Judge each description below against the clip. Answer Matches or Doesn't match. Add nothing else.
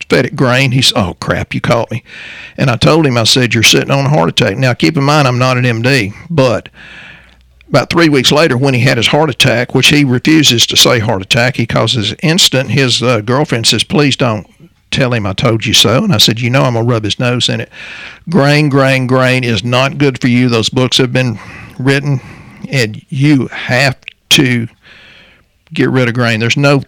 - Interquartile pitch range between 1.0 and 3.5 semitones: Matches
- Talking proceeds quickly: Matches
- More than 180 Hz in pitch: Doesn't match